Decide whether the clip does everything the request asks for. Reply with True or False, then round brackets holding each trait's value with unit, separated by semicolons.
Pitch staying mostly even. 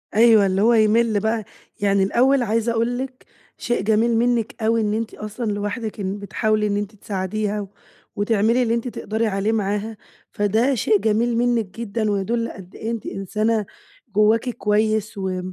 True (2.0 semitones)